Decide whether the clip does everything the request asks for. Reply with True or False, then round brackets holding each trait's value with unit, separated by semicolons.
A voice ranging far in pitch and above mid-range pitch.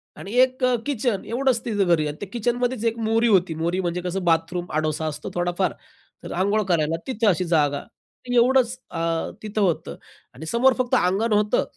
True (6.0 semitones; 195 Hz)